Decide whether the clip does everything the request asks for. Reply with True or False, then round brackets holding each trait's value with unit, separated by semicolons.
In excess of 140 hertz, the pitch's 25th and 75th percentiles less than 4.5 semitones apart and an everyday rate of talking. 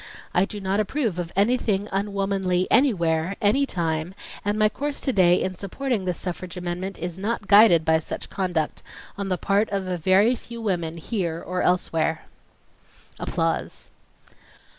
True (190 Hz; 3.0 semitones; 155 wpm)